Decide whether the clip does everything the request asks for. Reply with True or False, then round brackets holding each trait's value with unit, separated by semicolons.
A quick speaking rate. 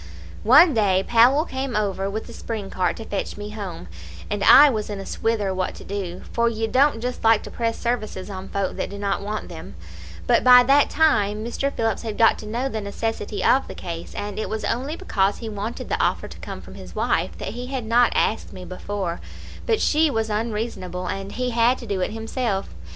True (220 wpm)